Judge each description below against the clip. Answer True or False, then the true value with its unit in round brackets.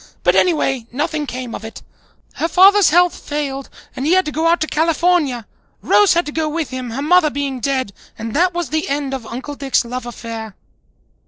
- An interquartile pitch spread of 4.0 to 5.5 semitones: True (4.6 semitones)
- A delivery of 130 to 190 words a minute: False (200 wpm)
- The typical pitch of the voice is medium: False (290 Hz)